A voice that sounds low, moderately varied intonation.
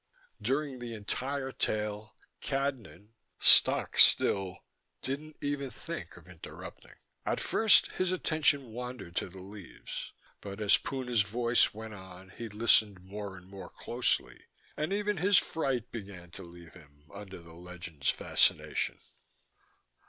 No: low, 105 Hz; wide, 6.2 semitones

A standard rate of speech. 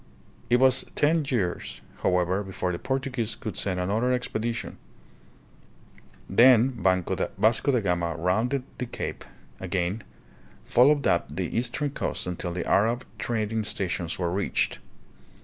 No: slow, 130 wpm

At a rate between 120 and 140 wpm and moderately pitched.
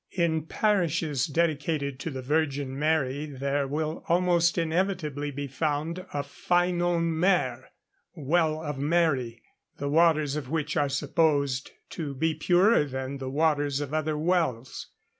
Yes: slow, 135 wpm; medium, 150 Hz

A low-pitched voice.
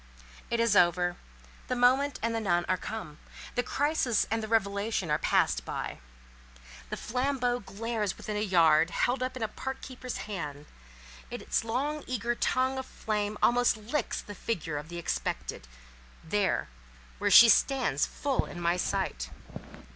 No: high, 215 Hz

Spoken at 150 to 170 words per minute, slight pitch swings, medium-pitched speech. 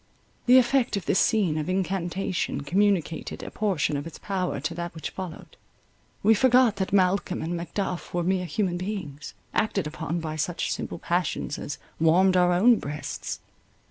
No: average, 165 wpm; average, 3.2 semitones; medium, 180 Hz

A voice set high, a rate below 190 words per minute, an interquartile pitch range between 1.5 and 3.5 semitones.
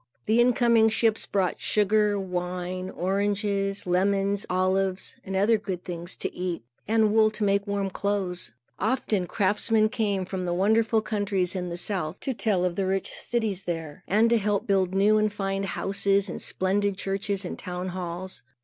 Yes: high, 195 Hz; average, 165 wpm; narrow, 2.4 semitones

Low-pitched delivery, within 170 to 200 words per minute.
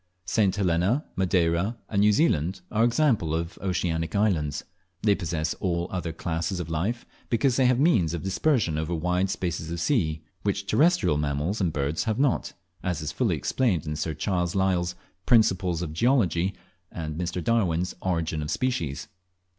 No: very low, 90 Hz; average, 160 wpm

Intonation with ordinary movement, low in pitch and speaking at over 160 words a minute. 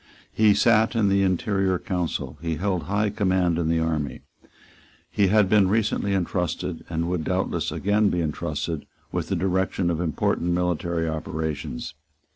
No: average, 3.2 semitones; very low, 90 Hz; average, 150 wpm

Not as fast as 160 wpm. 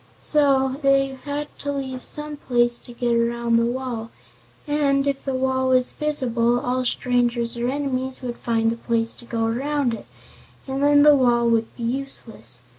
No: average, 175 wpm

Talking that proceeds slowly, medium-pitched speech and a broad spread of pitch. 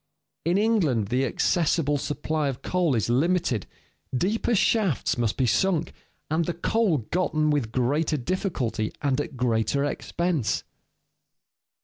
Yes: slow, 125 wpm; medium, 150 Hz; wide, 5.9 semitones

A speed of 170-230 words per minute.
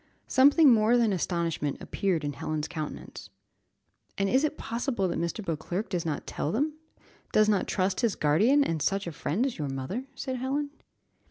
Yes: average, 175 wpm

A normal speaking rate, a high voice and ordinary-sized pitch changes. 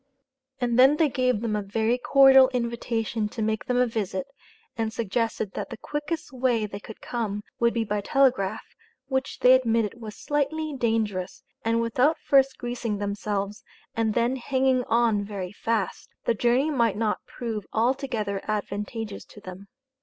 Yes: average, 160 wpm; high, 230 Hz; average, 3.4 semitones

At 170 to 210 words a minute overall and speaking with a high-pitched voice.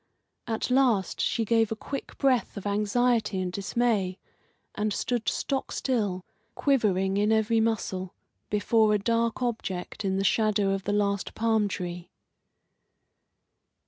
No: slow, 135 wpm; high, 210 Hz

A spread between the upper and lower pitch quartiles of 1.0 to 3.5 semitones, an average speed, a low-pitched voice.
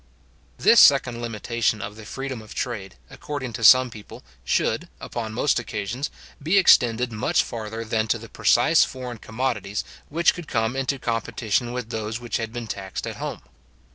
Yes: average, 2.8 semitones; average, 170 wpm; low, 115 Hz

